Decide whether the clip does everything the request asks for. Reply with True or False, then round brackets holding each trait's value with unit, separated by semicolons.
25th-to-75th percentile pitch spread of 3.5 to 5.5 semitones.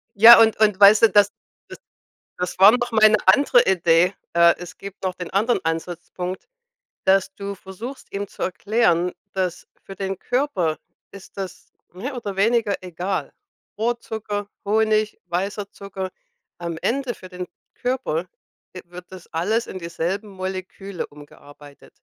False (3.1 semitones)